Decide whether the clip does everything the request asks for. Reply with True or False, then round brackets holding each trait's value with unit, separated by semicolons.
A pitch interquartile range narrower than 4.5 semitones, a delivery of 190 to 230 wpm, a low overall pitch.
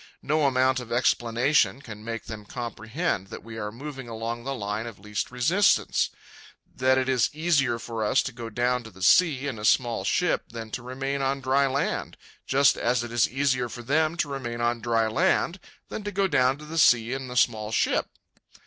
True (3.2 semitones; 205 wpm; 125 Hz)